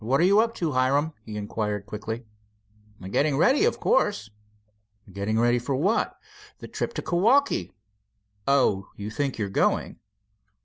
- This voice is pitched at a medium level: No, low, 130 Hz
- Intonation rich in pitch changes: Yes, wide, 8.5 semitones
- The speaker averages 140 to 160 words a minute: Yes, average, 145 wpm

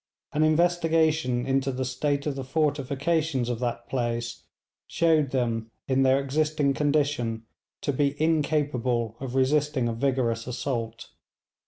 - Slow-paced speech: Yes, slow, 130 wpm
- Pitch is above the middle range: No, low, 135 Hz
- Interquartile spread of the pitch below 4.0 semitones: Yes, average, 3.6 semitones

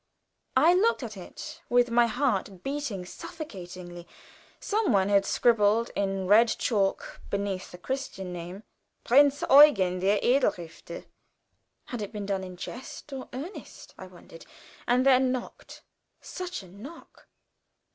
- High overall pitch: Yes, high, 220 Hz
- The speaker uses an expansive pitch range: Yes, wide, 6.1 semitones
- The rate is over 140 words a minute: No, slow, 135 wpm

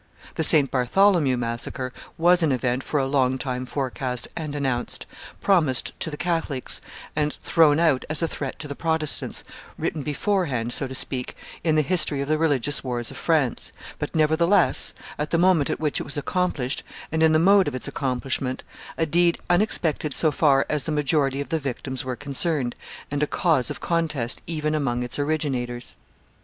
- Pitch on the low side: No, medium, 145 Hz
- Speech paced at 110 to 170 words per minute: No, average, 180 wpm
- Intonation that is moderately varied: Yes, average, 3.6 semitones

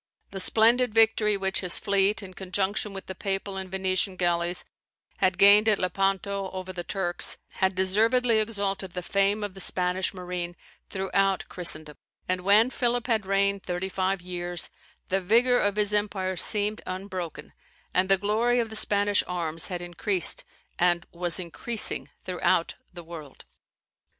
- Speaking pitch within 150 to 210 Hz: Yes, high, 190 Hz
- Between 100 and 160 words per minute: Yes, average, 155 wpm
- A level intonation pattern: Yes, narrow, 2.3 semitones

